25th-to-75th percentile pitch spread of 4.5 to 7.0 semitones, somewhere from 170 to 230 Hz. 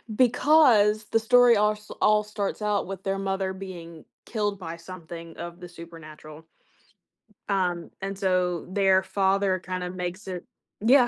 No: average, 3.1 semitones; high, 190 Hz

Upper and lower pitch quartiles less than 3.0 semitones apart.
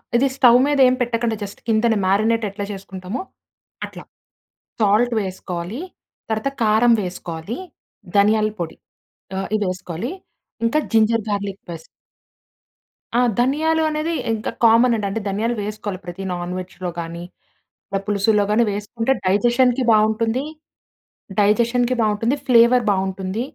No: average, 3.5 semitones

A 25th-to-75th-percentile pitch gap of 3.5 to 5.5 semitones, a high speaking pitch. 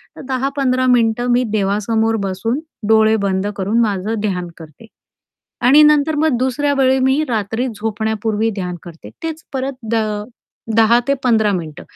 Yes: average, 3.9 semitones; high, 225 Hz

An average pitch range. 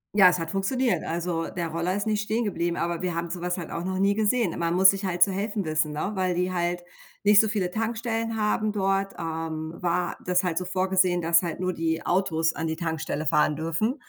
Yes: average, 3.0 semitones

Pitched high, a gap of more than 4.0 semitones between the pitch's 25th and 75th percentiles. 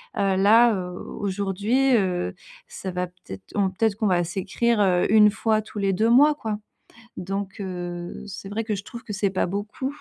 No: high, 200 Hz; average, 2.9 semitones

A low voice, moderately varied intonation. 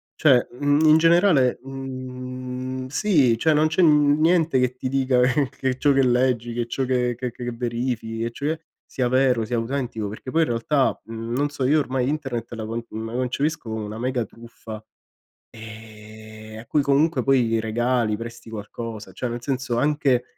Yes: low, 125 Hz; average, 3.0 semitones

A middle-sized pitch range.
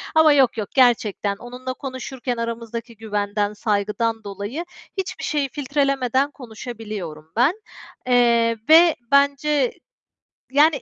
Yes: average, 4.3 semitones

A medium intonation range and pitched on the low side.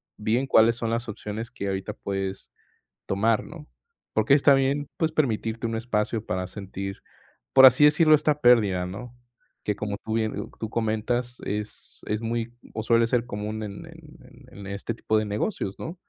Yes: average, 3.0 semitones; low, 110 Hz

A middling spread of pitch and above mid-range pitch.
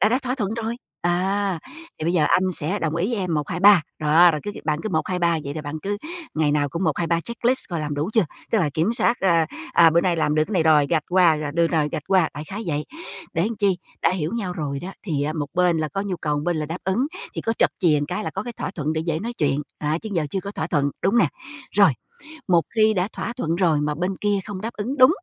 No: average, 4.5 semitones; medium, 175 Hz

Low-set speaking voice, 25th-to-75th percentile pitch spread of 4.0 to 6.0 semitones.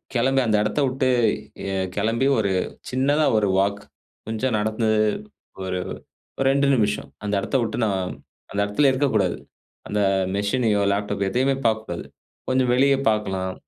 Yes: low, 110 Hz; average, 4.3 semitones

